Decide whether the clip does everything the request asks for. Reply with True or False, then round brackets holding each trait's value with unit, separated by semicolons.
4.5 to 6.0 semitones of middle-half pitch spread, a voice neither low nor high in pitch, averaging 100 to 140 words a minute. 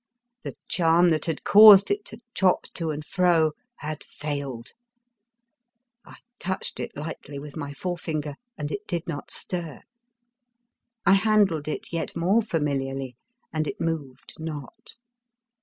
False (3.9 semitones; 160 Hz; 135 wpm)